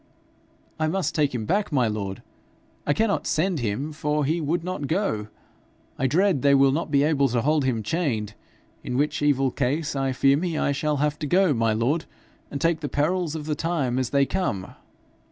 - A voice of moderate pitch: Yes, medium, 145 Hz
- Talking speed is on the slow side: No, average, 200 wpm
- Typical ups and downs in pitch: Yes, average, 3.4 semitones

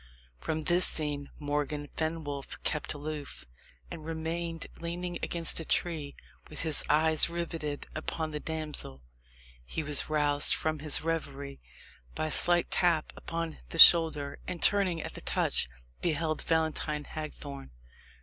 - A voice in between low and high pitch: Yes, medium, 155 Hz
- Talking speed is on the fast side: No, slow, 135 wpm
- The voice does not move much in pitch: Yes, narrow, 2.0 semitones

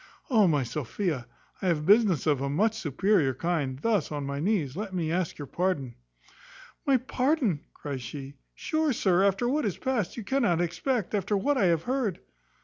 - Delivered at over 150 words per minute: Yes, average, 180 wpm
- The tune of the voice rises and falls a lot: Yes, wide, 7.0 semitones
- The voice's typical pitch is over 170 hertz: Yes, medium, 185 Hz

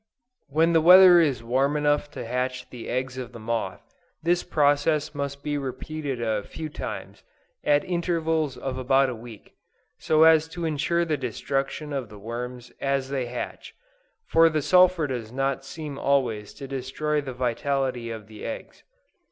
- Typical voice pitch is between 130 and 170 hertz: Yes, medium, 140 Hz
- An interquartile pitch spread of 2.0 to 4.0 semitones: Yes, average, 3.7 semitones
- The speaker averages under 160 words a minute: No, average, 165 wpm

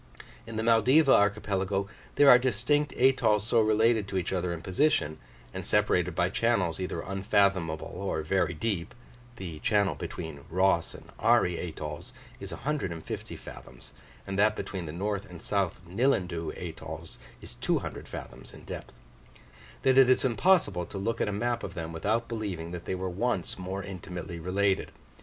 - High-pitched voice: No, very low, 95 Hz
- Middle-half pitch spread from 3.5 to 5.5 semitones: Yes, average, 4.5 semitones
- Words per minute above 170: No, average, 160 wpm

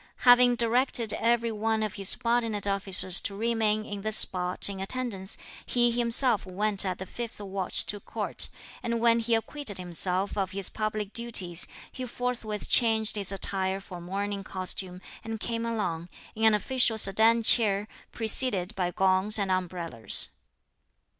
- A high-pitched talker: Yes, high, 210 Hz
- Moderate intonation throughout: Yes, average, 3.3 semitones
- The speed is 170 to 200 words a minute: No, average, 155 wpm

